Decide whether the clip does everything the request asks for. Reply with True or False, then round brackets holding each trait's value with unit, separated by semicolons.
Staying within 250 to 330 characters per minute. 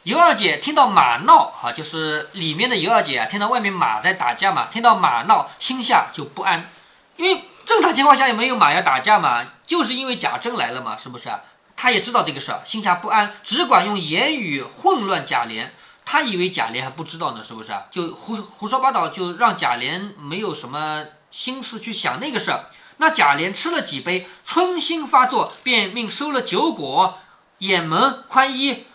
True (290 characters per minute)